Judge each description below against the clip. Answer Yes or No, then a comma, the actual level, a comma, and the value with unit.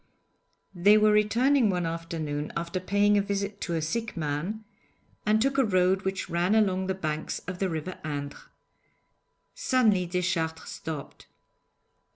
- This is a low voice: No, medium, 185 Hz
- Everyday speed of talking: Yes, average, 145 wpm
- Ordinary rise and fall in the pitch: Yes, average, 4.1 semitones